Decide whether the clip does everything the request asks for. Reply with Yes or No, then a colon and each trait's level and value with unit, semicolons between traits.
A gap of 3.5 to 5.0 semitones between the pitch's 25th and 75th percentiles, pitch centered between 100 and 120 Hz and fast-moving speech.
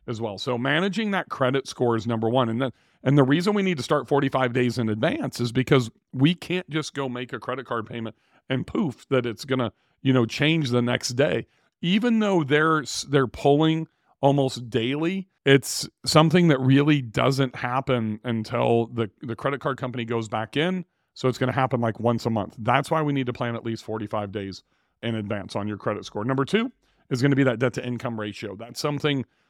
No: average, 3.8 semitones; low, 130 Hz; fast, 210 wpm